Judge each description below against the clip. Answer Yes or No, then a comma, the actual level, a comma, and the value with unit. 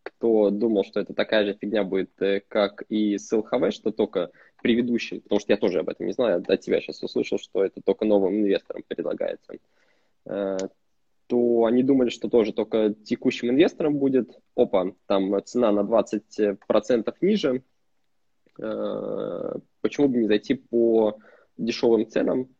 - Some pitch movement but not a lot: Yes, average, 3.8 semitones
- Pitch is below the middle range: Yes, low, 115 Hz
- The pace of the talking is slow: No, average, 150 wpm